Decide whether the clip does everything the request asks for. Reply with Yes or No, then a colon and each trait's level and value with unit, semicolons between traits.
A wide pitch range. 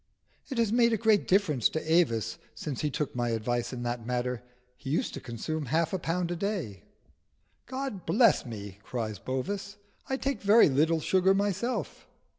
Yes: wide, 8.7 semitones